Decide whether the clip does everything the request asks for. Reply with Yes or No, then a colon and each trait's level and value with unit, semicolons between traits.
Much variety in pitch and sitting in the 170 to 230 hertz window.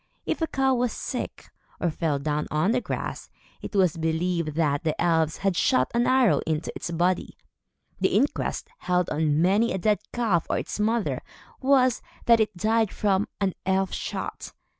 Yes: wide, 5.8 semitones; high, 190 Hz